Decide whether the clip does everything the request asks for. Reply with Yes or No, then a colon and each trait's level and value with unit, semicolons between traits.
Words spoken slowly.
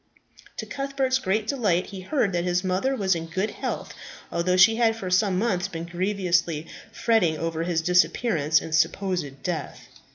No: average, 165 wpm